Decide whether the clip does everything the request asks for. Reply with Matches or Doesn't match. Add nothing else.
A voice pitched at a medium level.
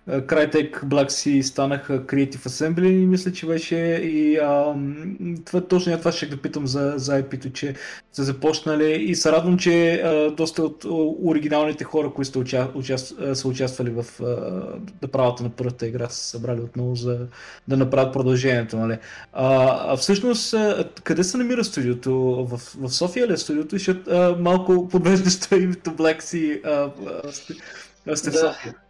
Matches